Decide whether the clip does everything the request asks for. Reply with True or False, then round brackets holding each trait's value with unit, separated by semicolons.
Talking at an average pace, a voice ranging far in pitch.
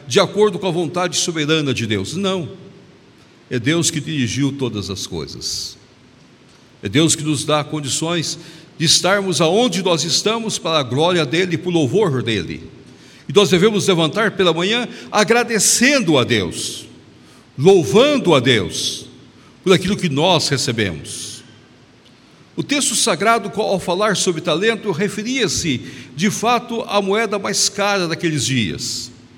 True (140 wpm; 6.8 semitones)